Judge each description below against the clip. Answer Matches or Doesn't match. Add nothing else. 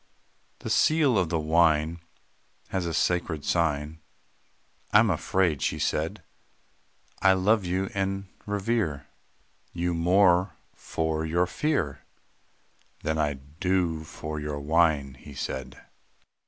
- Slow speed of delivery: Matches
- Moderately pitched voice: Doesn't match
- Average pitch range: Matches